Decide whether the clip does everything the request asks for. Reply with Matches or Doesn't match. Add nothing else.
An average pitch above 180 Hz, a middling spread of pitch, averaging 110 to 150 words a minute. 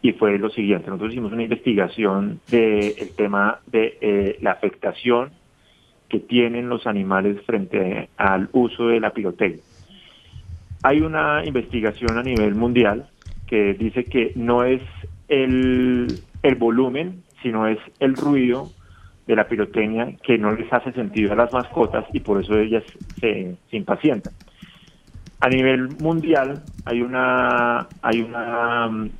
Doesn't match